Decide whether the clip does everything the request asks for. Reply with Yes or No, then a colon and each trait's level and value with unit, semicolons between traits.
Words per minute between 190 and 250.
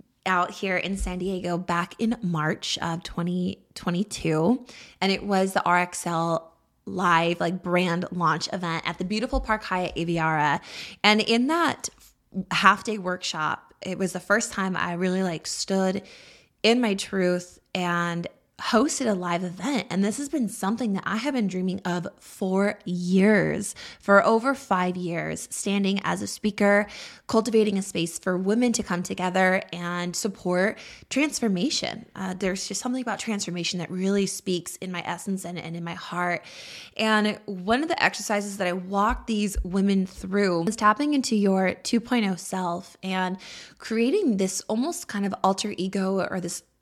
No: average, 160 wpm